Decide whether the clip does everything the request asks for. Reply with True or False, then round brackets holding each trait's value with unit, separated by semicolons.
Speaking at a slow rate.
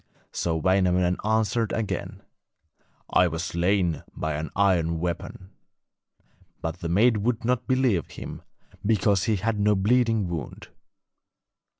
True (120 wpm)